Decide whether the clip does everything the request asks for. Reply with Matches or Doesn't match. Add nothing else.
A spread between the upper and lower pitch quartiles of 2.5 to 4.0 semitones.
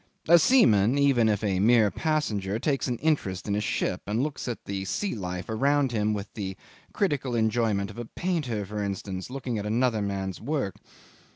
Doesn't match